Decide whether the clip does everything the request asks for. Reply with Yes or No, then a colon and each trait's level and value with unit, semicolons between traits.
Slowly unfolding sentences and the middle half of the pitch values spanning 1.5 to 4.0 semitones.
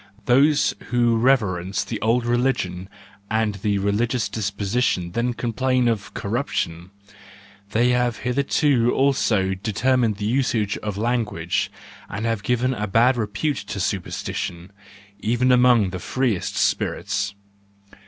Yes: slow, 125 wpm; average, 3.7 semitones